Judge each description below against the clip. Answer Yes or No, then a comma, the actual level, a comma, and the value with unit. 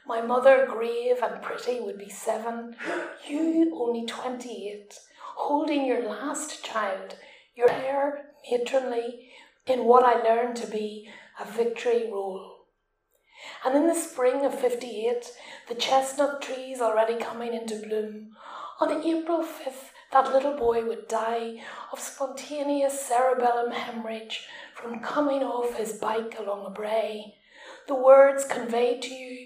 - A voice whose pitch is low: No, very high, 250 Hz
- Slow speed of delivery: Yes, slow, 130 wpm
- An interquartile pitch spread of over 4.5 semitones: No, average, 3.6 semitones